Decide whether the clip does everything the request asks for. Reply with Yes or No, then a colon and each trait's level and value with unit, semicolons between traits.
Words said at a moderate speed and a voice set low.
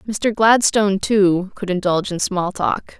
No: average, 160 wpm; high, 195 Hz